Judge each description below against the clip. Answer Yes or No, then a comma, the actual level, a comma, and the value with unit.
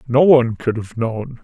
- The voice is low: Yes, low, 120 Hz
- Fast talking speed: Yes, fast, 210 wpm